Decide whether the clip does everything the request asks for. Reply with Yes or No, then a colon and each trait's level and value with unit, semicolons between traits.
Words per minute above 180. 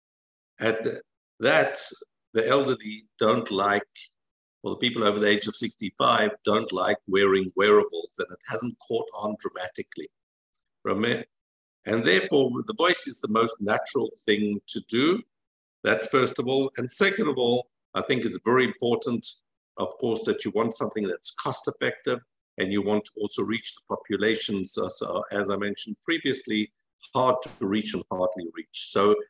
No: average, 160 wpm